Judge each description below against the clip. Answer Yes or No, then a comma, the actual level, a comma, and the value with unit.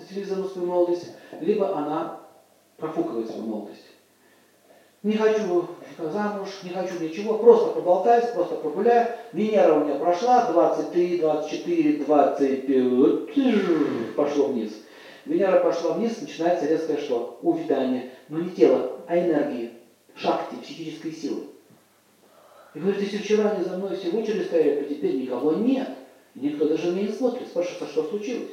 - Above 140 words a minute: No, average, 135 wpm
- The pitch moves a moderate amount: No, wide, 6.0 semitones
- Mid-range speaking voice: Yes, medium, 180 Hz